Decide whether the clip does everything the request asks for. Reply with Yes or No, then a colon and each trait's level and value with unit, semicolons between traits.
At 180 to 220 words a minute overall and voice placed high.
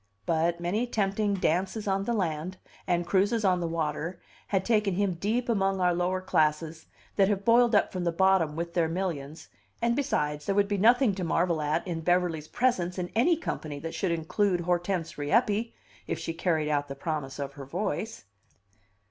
No: average, 185 wpm; medium, 180 Hz